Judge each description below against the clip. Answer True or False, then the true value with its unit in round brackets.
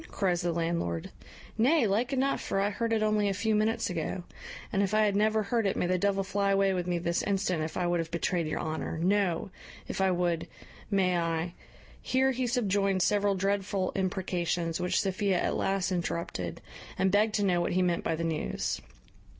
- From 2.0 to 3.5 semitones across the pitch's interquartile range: True (2.8 semitones)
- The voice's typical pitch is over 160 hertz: True (190 Hz)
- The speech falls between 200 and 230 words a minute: True (205 wpm)